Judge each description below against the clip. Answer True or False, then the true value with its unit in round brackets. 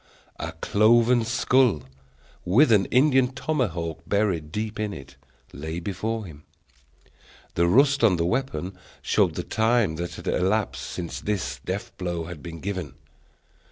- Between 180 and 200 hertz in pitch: False (100 Hz)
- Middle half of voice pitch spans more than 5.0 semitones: True (5.5 semitones)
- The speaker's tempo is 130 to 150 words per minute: True (140 wpm)